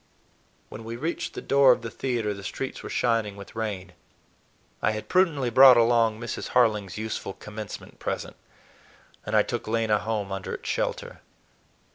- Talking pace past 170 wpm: No, average, 160 wpm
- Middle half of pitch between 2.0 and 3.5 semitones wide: Yes, narrow, 2.6 semitones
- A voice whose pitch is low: Yes, low, 110 Hz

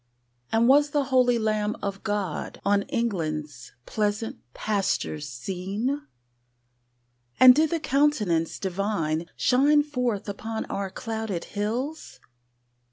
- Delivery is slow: Yes, slow, 105 wpm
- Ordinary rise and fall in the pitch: Yes, average, 4.9 semitones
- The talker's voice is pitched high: Yes, high, 215 Hz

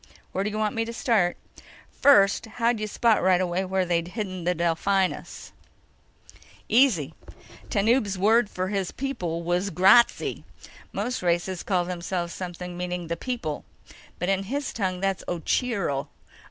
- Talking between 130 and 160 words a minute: Yes, average, 145 wpm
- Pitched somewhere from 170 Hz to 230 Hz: Yes, high, 190 Hz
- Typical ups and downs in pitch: Yes, average, 3.4 semitones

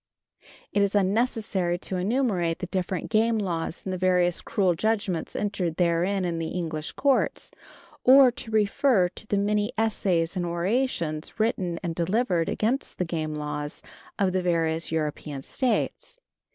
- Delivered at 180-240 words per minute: No, average, 150 wpm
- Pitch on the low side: No, medium, 185 Hz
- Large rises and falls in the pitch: No, average, 4.3 semitones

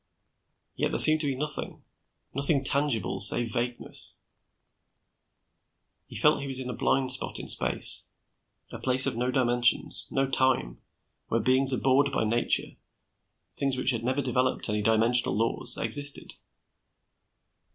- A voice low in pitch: Yes, low, 130 Hz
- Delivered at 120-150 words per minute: Yes, average, 140 wpm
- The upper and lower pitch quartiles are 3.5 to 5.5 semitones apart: No, narrow, 2.5 semitones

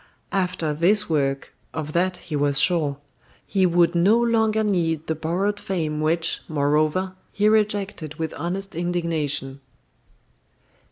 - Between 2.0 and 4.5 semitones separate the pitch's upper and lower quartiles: Yes, average, 4.0 semitones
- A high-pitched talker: No, medium, 170 Hz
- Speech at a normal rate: No, slow, 125 wpm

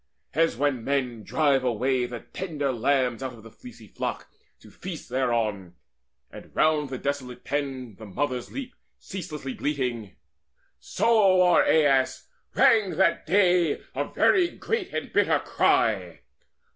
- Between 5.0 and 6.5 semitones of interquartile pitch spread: Yes, wide, 5.6 semitones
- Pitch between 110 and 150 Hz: Yes, medium, 140 Hz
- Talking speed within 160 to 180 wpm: No, slow, 135 wpm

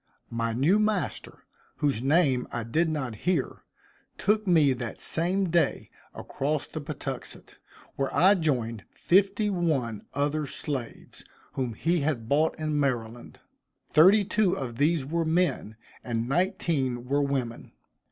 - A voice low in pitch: No, medium, 145 Hz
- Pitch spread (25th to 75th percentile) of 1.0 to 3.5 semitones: No, wide, 5.5 semitones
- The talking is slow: Yes, slow, 130 wpm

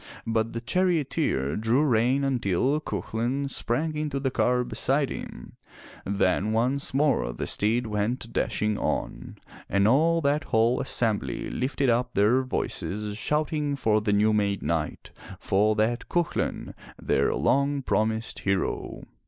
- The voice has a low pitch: Yes, low, 120 Hz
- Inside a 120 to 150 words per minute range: Yes, slow, 135 wpm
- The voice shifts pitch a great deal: No, average, 4.6 semitones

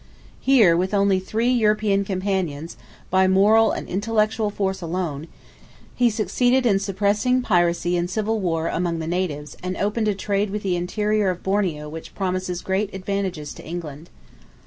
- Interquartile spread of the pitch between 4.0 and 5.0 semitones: No, average, 3.2 semitones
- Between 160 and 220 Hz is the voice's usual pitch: Yes, high, 190 Hz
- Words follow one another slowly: No, average, 155 wpm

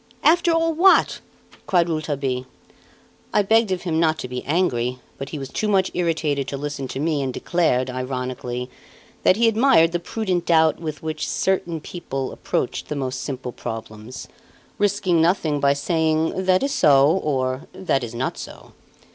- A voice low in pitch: No, medium, 155 Hz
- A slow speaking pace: No, average, 165 wpm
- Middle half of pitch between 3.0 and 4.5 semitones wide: No, wide, 5.5 semitones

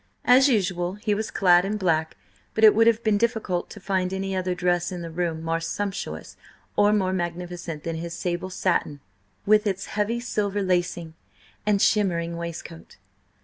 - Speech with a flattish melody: No, average, 3.2 semitones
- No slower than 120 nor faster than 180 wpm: Yes, average, 170 wpm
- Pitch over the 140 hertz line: Yes, medium, 185 Hz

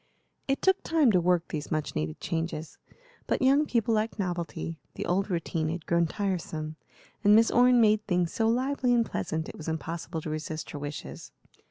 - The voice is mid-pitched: Yes, medium, 180 Hz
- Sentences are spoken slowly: No, average, 185 wpm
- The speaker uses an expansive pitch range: Yes, wide, 6.0 semitones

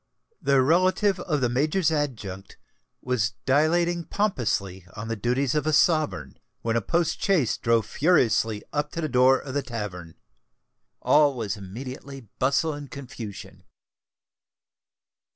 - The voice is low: Yes, low, 130 Hz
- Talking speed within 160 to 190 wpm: No, slow, 135 wpm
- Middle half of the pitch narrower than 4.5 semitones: No, wide, 5.4 semitones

